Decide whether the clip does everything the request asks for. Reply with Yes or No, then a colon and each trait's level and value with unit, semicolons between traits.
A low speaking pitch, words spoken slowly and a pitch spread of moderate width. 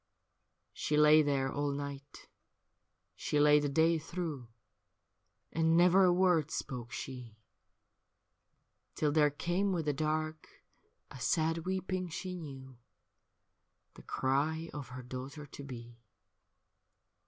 No: medium, 150 Hz; slow, 120 wpm; average, 3.3 semitones